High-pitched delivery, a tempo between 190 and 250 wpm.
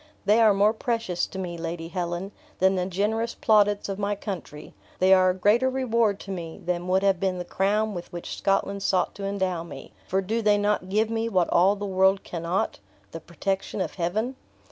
Yes: high, 195 Hz; fast, 205 wpm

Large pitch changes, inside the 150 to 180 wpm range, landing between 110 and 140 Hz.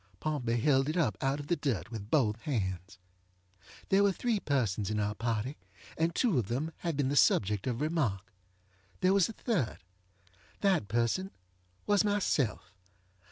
Yes: wide, 7.5 semitones; average, 160 wpm; low, 135 Hz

